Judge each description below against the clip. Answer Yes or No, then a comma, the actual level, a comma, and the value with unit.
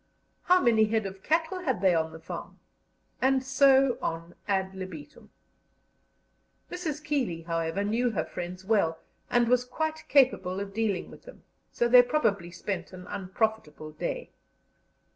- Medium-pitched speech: No, high, 210 Hz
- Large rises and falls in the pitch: Yes, wide, 6.6 semitones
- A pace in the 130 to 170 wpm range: Yes, average, 145 wpm